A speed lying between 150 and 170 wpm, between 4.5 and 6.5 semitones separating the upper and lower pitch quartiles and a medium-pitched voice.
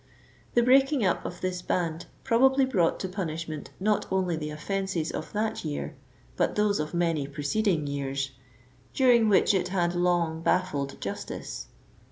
Yes: average, 160 wpm; average, 5.1 semitones; medium, 180 Hz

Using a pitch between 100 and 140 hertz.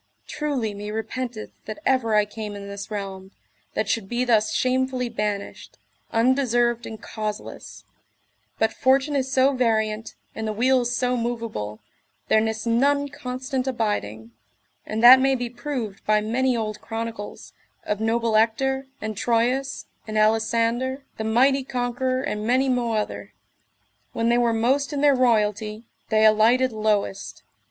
No: high, 230 Hz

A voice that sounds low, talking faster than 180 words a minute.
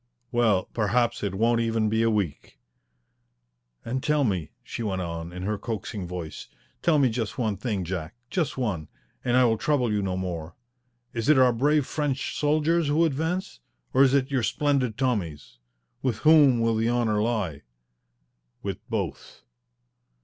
No: low, 115 Hz; average, 165 wpm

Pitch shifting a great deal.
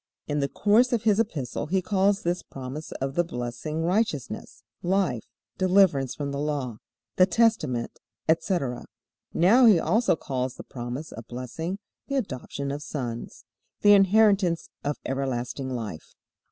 Yes: wide, 7.0 semitones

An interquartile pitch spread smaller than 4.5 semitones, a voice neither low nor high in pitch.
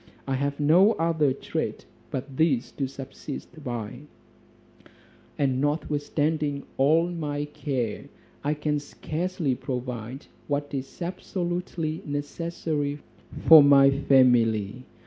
Yes: average, 2.8 semitones; medium, 145 Hz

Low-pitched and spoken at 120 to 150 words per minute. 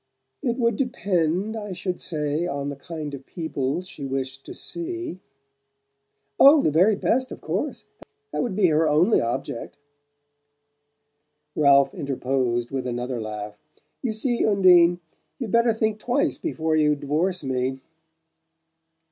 No: medium, 165 Hz; slow, 135 wpm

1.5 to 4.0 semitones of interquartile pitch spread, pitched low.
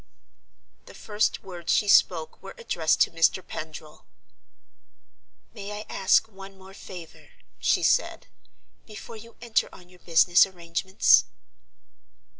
No: average, 3.4 semitones; high, 190 Hz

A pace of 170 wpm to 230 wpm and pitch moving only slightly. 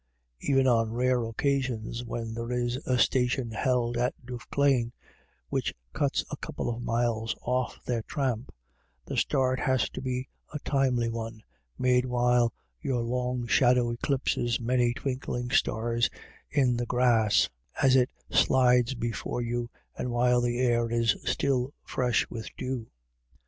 No: average, 140 wpm; narrow, 1.4 semitones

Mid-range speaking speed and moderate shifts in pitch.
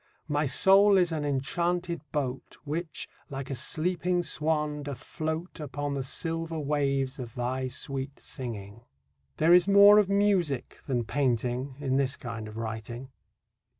Yes: average, 145 wpm; average, 4.4 semitones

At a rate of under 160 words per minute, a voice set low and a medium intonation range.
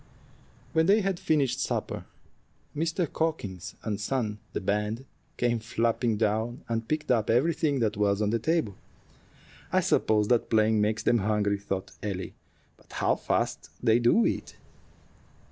Yes: average, 145 wpm; low, 115 Hz; average, 4.3 semitones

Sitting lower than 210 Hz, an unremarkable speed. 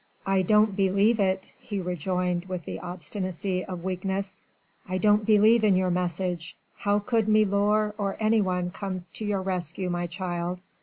Yes: high, 190 Hz; average, 155 wpm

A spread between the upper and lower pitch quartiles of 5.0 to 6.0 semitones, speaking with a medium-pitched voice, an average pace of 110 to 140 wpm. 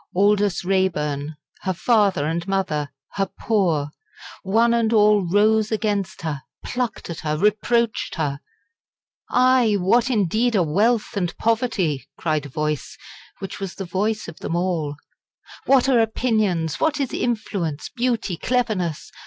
No: average, 5.3 semitones; high, 195 Hz; slow, 135 wpm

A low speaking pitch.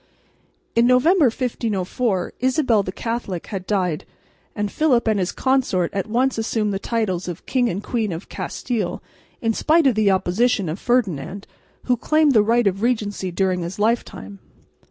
No: high, 215 Hz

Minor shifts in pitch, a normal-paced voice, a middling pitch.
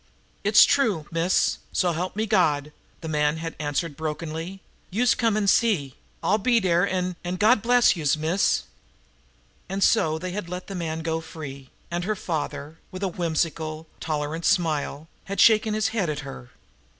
No: average, 4.1 semitones; average, 170 wpm; medium, 170 Hz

